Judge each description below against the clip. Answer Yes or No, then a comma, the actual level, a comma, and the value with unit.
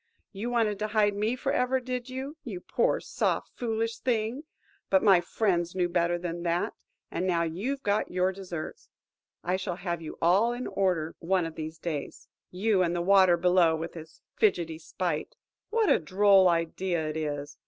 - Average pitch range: Yes, average, 4.1 semitones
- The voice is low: No, medium, 185 Hz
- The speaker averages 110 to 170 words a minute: No, average, 180 wpm